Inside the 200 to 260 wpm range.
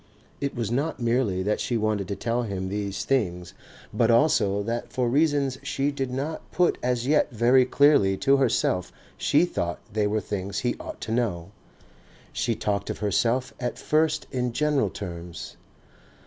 No: average, 165 wpm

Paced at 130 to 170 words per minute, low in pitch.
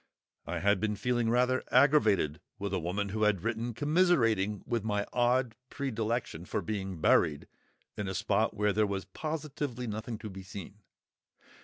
Yes: average, 160 wpm; low, 110 Hz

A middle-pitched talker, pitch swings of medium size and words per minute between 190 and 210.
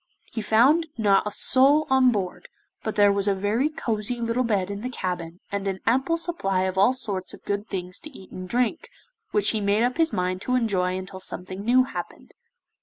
No: high, 210 Hz; average, 4.8 semitones; fast, 205 wpm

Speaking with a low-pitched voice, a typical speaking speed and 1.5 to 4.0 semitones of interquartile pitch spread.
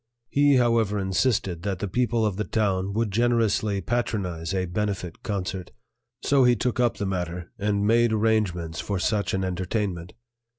Yes: low, 100 Hz; average, 160 wpm; average, 3.6 semitones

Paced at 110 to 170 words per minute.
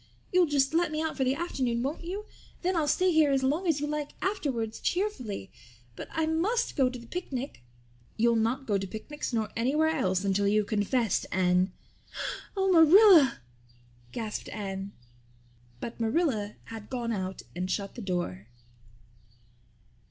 Yes: average, 160 wpm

